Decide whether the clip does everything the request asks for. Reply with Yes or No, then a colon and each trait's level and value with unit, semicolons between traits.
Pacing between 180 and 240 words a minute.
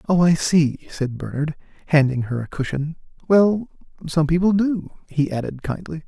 No: average, 160 wpm